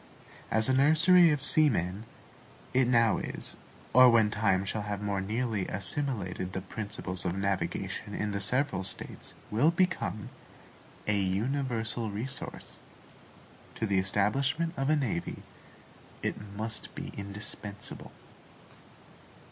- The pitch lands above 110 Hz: No, low, 105 Hz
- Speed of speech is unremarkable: No, slow, 120 wpm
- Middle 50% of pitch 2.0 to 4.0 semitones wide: No, average, 5.0 semitones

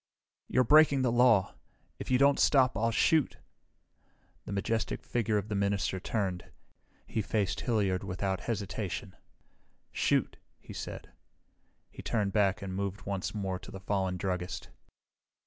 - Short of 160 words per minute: Yes, average, 140 wpm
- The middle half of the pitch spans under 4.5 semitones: Yes, average, 3.4 semitones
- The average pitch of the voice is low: Yes, low, 100 Hz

